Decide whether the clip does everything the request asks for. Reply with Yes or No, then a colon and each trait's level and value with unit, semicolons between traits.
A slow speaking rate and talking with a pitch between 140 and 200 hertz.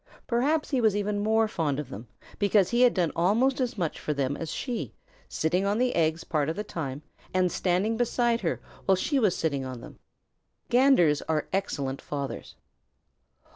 No: average, 180 wpm; medium, 185 Hz